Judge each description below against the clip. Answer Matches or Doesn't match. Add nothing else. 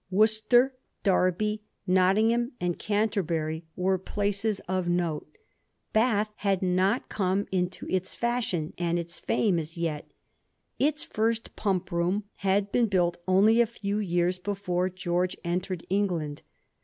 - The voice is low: Doesn't match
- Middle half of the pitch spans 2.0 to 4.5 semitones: Matches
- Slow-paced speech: Matches